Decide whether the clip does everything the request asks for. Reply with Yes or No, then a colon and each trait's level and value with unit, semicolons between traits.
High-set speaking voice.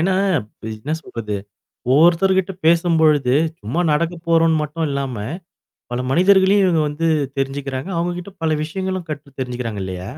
No: medium, 160 Hz